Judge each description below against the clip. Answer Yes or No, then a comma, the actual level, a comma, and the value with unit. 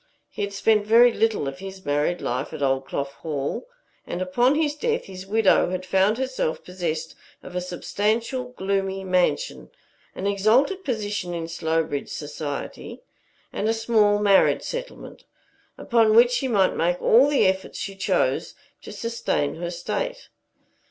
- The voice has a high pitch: Yes, high, 195 Hz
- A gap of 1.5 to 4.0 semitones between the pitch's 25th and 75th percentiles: No, average, 4.9 semitones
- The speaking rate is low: No, average, 150 wpm